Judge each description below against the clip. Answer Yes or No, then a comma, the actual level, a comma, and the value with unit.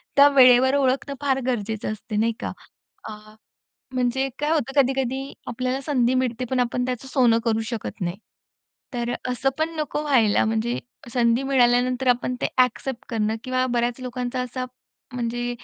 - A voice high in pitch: Yes, very high, 250 Hz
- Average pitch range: No, narrow, 2.0 semitones